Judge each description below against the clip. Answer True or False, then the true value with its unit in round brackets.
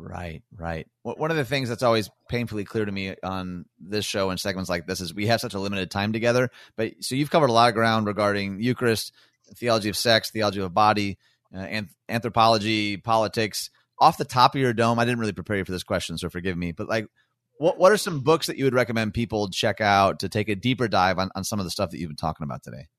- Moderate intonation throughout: True (3.6 semitones)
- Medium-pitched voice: False (105 Hz)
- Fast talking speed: True (250 wpm)